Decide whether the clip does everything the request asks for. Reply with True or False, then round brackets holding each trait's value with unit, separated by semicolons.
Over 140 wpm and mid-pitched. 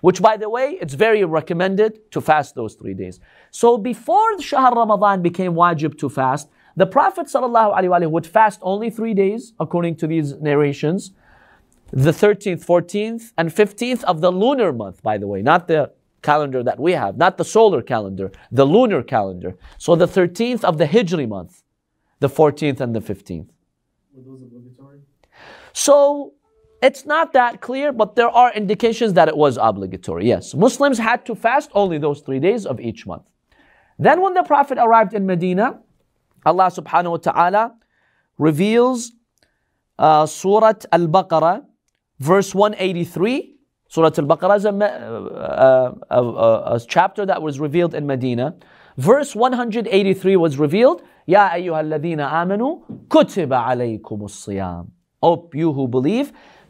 True (150 wpm; 180 Hz)